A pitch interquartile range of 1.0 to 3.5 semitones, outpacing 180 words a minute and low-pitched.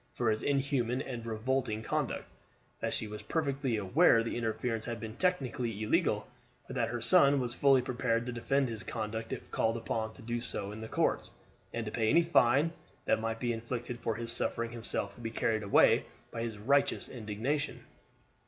Yes: narrow, 2.5 semitones; average, 190 wpm; low, 115 Hz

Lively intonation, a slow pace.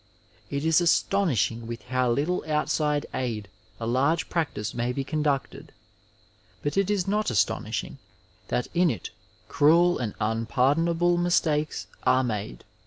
Yes: wide, 6.0 semitones; slow, 130 wpm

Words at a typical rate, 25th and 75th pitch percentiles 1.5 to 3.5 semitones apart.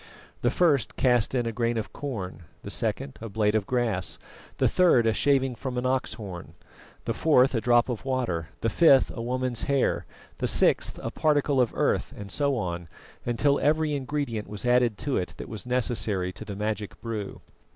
No: average, 190 wpm; average, 3.9 semitones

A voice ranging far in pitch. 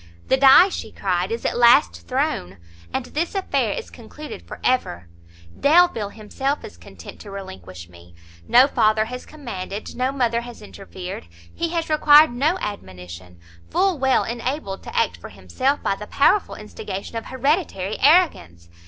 Yes: wide, 7.6 semitones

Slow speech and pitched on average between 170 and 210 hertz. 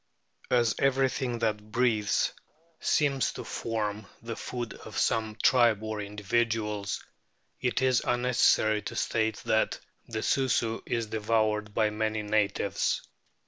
No: slow, 125 wpm; low, 110 Hz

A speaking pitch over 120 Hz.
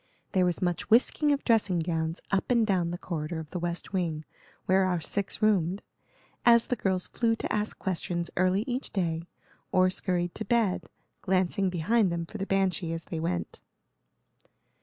Yes: medium, 185 Hz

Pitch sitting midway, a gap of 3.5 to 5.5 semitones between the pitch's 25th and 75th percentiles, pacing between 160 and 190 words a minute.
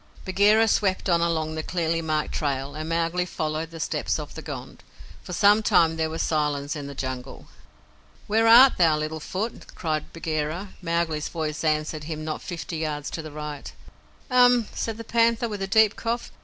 Yes: medium, 165 Hz; average, 4.6 semitones; average, 185 wpm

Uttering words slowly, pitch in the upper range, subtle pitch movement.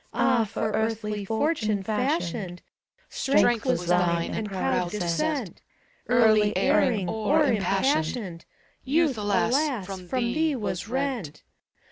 No: slow, 105 wpm; high, 220 Hz; average, 5.3 semitones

